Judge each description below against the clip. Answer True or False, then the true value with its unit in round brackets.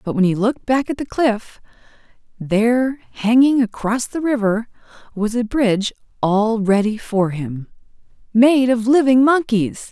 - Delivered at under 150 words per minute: True (140 wpm)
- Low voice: False (230 Hz)